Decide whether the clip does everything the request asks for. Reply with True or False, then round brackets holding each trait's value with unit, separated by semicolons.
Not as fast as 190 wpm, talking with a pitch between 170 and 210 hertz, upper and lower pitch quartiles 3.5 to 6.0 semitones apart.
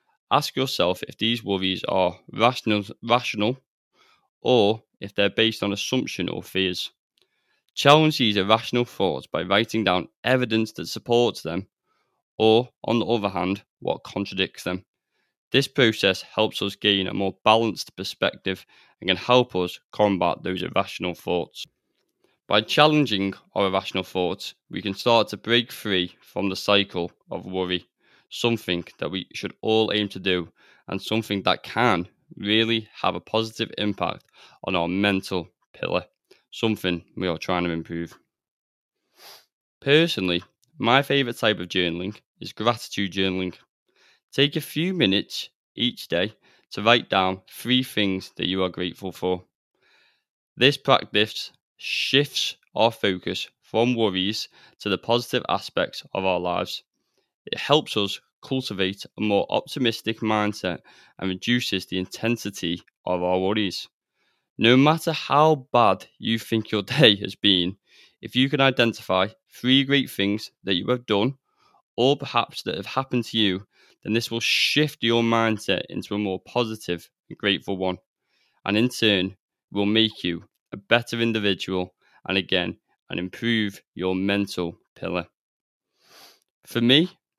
False (145 wpm; 105 Hz; 4.0 semitones)